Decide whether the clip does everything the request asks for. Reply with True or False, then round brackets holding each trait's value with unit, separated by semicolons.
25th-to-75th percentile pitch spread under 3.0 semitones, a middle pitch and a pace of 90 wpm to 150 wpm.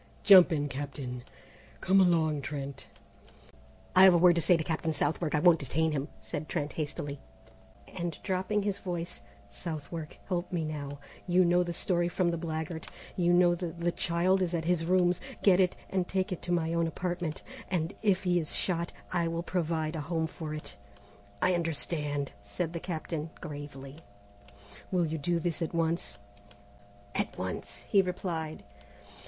False (2.5 semitones; 170 Hz; 170 wpm)